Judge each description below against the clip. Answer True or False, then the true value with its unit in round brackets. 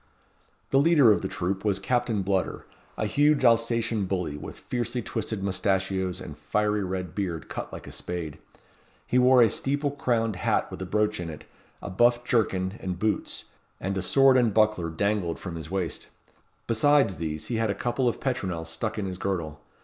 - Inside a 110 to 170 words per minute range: False (185 wpm)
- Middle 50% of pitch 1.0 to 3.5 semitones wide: False (4.5 semitones)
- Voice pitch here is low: True (100 Hz)